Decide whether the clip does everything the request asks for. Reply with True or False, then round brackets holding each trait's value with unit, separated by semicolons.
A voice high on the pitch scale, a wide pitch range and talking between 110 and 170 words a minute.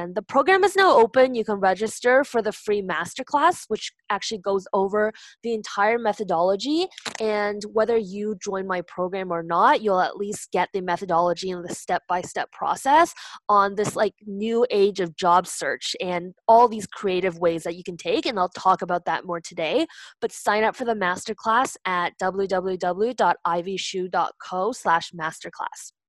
False (200 Hz; 3.5 semitones; 160 wpm)